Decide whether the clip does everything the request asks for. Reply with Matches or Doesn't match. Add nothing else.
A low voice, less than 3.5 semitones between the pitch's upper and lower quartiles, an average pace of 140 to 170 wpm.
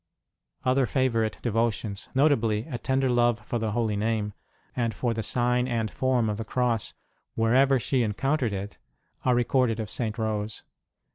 Matches